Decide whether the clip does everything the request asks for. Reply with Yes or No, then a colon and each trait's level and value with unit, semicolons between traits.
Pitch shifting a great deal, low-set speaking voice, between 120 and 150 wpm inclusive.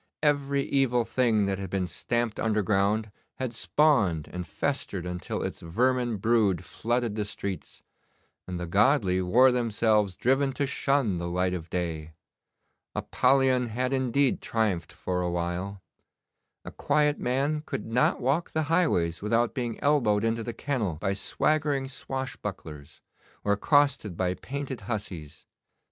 Yes: wide, 6.1 semitones; low, 115 Hz; average, 140 wpm